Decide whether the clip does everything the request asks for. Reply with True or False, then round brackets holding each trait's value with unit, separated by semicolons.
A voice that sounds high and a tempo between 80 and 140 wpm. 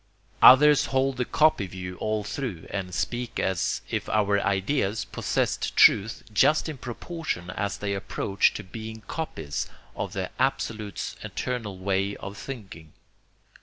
False (105 Hz; 135 wpm)